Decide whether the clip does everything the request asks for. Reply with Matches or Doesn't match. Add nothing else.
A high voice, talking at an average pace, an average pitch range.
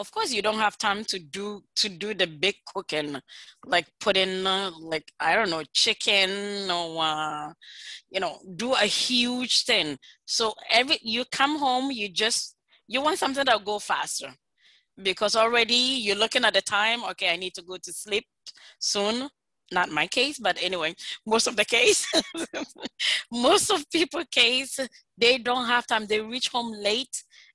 Matches